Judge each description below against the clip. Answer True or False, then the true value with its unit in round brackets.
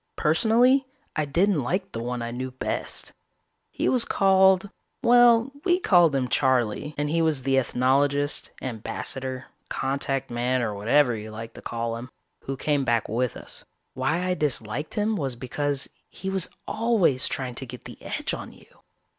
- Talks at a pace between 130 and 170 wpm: True (165 wpm)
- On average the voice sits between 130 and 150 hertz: True (140 Hz)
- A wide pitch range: True (6.6 semitones)